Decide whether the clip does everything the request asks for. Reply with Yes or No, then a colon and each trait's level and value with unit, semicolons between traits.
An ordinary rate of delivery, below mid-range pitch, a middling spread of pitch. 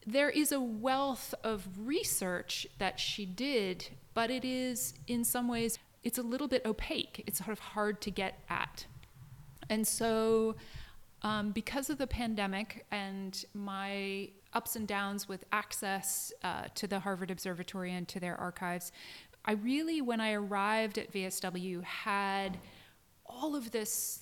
No: average, 150 wpm; high, 210 Hz; average, 3.6 semitones